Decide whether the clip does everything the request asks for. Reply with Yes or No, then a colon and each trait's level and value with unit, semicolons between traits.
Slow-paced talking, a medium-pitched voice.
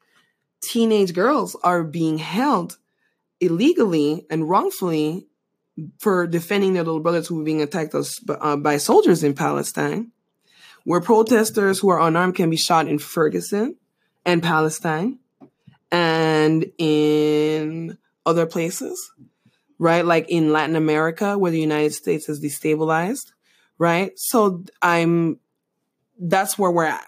Yes: slow, 120 wpm; medium, 170 Hz